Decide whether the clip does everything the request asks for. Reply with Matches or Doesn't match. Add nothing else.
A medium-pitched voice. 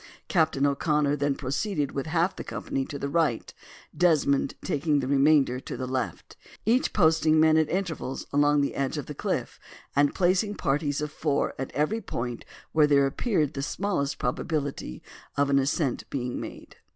Matches